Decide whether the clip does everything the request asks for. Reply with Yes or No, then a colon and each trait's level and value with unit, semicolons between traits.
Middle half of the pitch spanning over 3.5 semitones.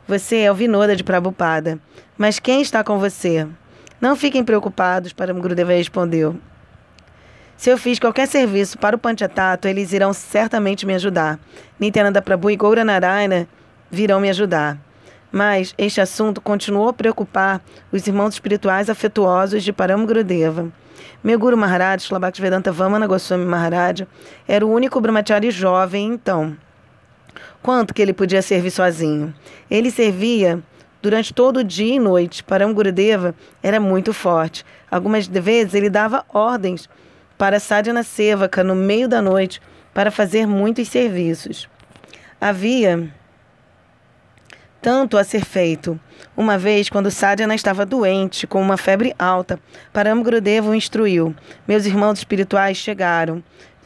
No: average, 2.8 semitones